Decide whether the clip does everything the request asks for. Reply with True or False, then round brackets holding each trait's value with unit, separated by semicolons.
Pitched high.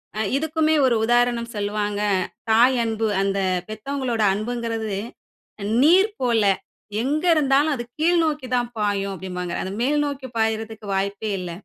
True (235 Hz)